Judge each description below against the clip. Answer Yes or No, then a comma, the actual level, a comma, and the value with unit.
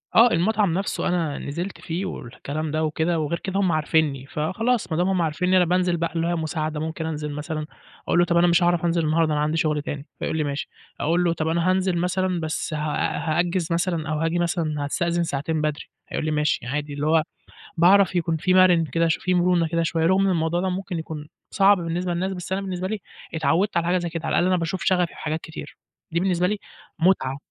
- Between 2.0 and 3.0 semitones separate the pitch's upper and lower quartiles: Yes, narrow, 2.5 semitones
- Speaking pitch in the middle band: Yes, medium, 170 Hz